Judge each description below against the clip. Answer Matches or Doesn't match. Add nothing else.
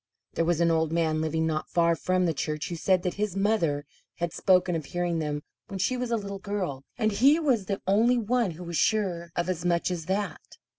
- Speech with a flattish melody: Doesn't match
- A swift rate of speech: Matches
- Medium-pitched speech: Matches